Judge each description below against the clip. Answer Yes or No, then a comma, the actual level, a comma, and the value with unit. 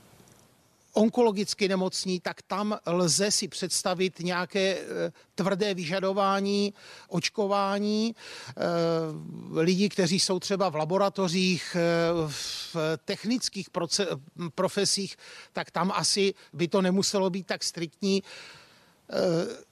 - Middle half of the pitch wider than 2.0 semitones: Yes, narrow, 2.4 semitones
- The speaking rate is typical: No, slow, 90 wpm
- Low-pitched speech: No, high, 190 Hz